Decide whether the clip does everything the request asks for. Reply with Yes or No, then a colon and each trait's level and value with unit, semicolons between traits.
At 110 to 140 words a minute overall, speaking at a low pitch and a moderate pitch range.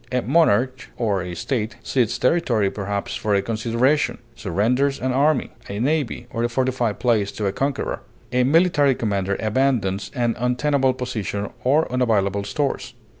No: average, 150 wpm; low, 120 Hz; average, 4.4 semitones